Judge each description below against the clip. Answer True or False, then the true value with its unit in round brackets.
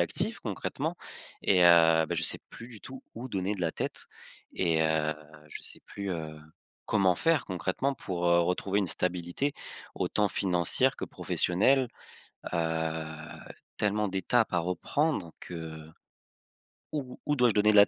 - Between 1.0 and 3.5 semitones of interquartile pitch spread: False (4.3 semitones)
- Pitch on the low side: True (90 Hz)